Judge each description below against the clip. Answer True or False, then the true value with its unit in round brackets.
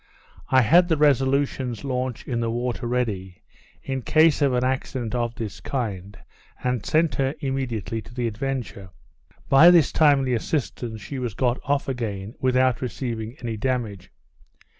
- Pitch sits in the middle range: False (125 Hz)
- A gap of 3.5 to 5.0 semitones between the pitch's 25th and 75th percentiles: False (3.0 semitones)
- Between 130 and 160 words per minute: True (150 wpm)